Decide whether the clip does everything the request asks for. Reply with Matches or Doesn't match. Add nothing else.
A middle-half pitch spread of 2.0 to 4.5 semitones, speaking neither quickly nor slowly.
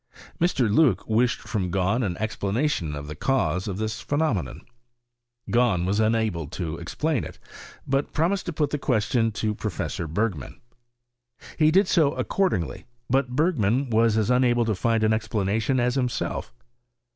Doesn't match